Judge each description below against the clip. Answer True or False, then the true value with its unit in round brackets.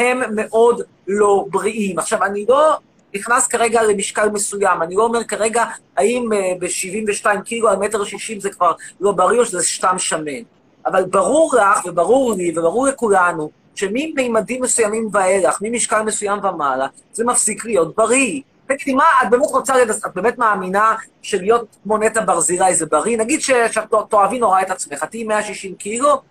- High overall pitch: True (215 Hz)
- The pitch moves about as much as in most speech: True (3.3 semitones)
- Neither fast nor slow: False (155 wpm)